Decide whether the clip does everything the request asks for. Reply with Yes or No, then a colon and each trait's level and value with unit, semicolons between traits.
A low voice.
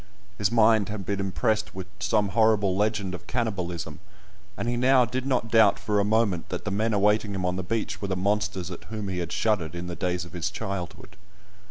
Yes: low, 100 Hz